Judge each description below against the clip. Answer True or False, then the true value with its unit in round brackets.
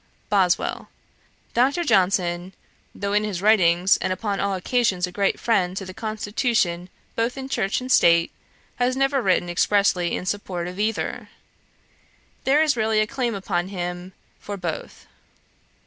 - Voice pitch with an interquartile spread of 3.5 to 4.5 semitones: True (4.1 semitones)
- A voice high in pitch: True (200 Hz)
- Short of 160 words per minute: True (145 wpm)